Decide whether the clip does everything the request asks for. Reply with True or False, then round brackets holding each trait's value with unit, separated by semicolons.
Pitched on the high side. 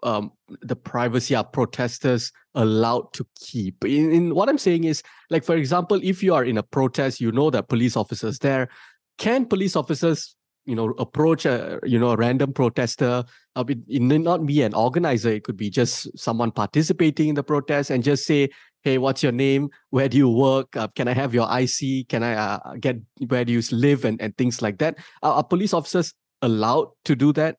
False (135 Hz)